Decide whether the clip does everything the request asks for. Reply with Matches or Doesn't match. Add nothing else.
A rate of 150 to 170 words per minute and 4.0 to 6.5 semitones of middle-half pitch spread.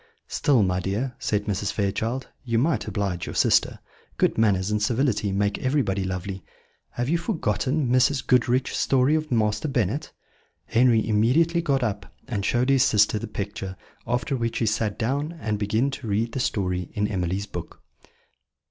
Matches